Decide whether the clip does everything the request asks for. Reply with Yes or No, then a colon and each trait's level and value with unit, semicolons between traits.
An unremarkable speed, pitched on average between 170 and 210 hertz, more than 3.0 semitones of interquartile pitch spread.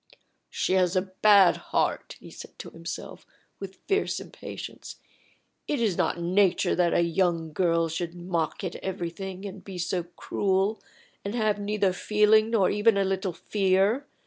No: average, 155 wpm; high, 190 Hz; average, 2.7 semitones